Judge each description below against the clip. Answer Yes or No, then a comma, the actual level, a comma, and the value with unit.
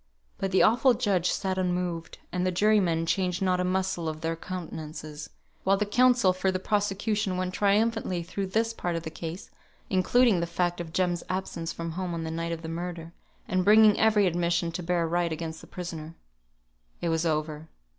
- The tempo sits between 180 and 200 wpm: Yes, average, 190 wpm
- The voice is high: No, medium, 180 Hz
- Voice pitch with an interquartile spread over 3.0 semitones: No, narrow, 2.6 semitones